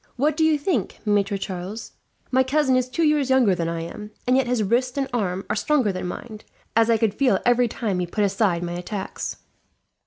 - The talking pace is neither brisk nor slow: No, fast, 215 wpm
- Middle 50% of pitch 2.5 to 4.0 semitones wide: No, average, 5.2 semitones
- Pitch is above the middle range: Yes, high, 225 Hz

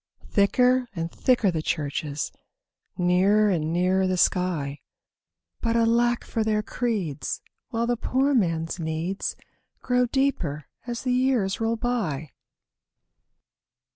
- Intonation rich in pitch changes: Yes, wide, 6.4 semitones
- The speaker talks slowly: Yes, slow, 110 wpm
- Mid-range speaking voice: No, high, 200 Hz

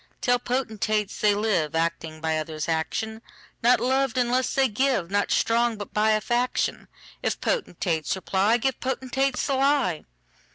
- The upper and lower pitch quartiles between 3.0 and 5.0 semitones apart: No, wide, 5.5 semitones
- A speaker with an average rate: No, slow, 120 wpm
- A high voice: Yes, high, 220 Hz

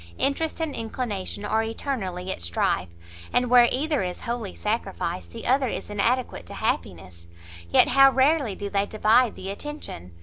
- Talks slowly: No, average, 160 wpm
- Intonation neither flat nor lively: No, wide, 5.8 semitones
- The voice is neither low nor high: No, high, 225 Hz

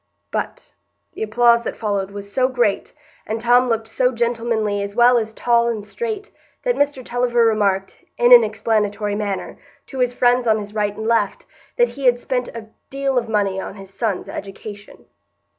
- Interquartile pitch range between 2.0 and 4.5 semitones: Yes, average, 2.8 semitones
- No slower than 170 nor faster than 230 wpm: Yes, average, 180 wpm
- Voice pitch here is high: Yes, high, 230 Hz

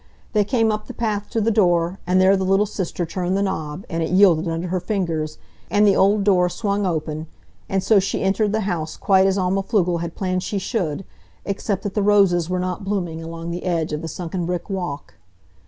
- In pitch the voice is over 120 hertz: Yes, medium, 185 Hz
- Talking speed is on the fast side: Yes, fast, 220 wpm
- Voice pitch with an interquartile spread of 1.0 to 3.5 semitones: Yes, average, 2.9 semitones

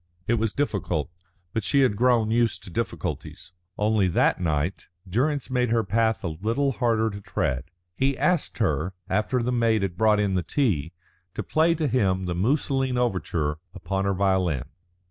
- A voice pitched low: Yes, low, 110 Hz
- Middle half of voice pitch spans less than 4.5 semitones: No, average, 4.9 semitones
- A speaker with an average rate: Yes, average, 170 wpm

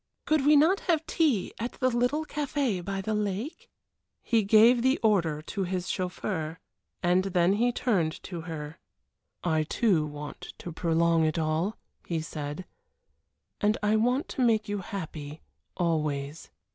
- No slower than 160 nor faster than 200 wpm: No, average, 150 wpm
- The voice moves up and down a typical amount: No, wide, 6.5 semitones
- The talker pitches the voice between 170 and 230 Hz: Yes, high, 190 Hz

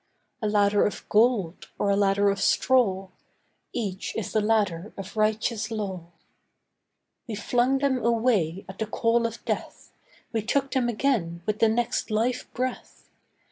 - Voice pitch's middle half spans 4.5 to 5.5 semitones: No, average, 3.1 semitones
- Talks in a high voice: Yes, high, 215 Hz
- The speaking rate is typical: Yes, average, 150 wpm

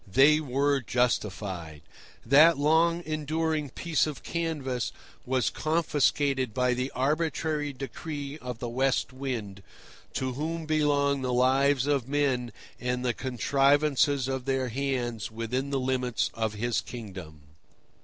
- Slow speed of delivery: Yes, slow, 125 wpm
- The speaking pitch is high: No, low, 135 Hz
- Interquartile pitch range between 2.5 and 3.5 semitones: Yes, average, 3.0 semitones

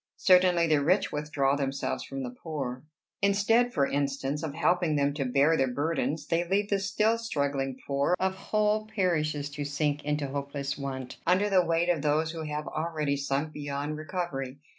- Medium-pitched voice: Yes, medium, 150 Hz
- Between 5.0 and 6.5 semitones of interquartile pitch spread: No, average, 4.0 semitones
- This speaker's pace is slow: No, average, 175 wpm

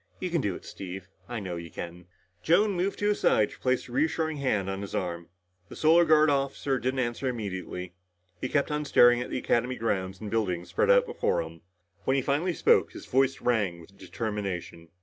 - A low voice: Yes, low, 120 Hz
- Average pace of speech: No, fast, 210 wpm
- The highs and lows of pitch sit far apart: Yes, wide, 7.2 semitones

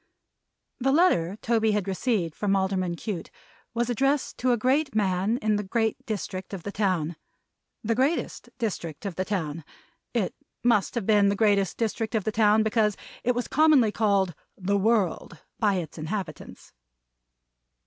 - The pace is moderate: Yes, average, 160 wpm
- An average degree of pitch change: Yes, average, 3.4 semitones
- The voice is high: Yes, high, 210 Hz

